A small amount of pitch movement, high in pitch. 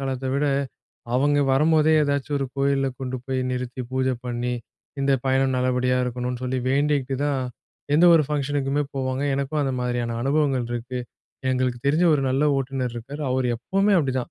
No: narrow, 2.0 semitones; low, 135 Hz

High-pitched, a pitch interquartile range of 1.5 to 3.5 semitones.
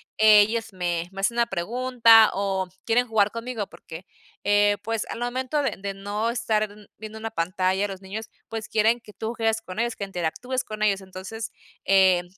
Yes: high, 215 Hz; average, 2.8 semitones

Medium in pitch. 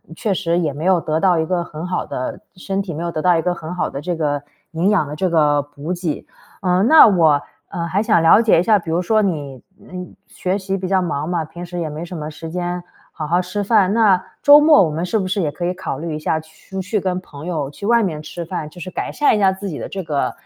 Yes: medium, 175 Hz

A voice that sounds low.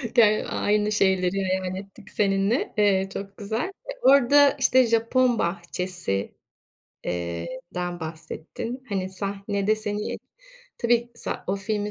No: high, 200 Hz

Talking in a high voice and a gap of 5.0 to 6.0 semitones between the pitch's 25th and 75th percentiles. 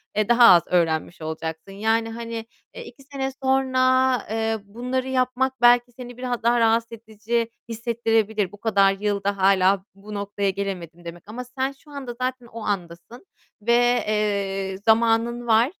No: high, 225 Hz; average, 3.6 semitones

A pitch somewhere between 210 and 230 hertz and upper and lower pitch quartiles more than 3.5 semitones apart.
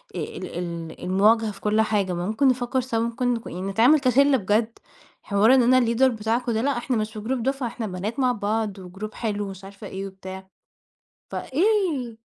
Yes: high, 220 Hz; average, 3.9 semitones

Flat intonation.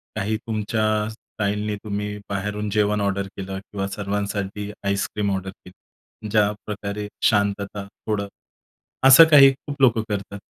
Yes: narrow, 1.1 semitones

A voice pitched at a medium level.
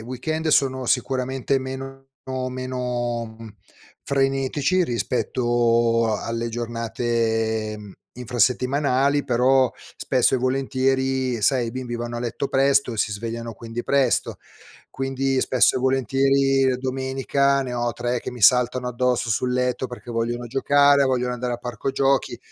No: low, 125 Hz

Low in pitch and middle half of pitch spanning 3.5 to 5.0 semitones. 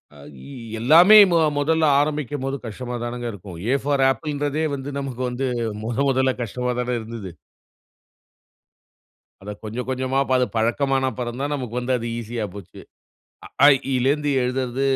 No: low, 130 Hz; average, 2.9 semitones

